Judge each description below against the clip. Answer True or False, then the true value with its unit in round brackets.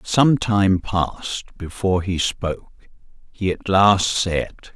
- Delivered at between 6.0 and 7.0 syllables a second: False (3.6 syllables/s)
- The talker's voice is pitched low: True (95 Hz)